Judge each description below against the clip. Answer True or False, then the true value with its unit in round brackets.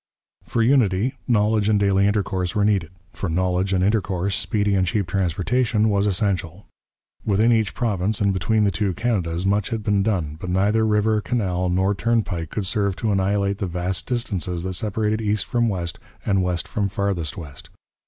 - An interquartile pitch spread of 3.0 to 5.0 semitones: False (2.6 semitones)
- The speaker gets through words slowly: False (175 wpm)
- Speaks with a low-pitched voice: True (100 Hz)